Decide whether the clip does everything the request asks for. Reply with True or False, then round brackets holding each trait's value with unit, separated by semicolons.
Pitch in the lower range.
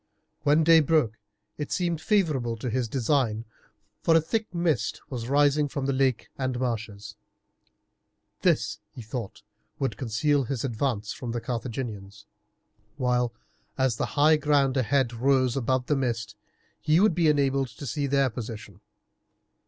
True (130 Hz)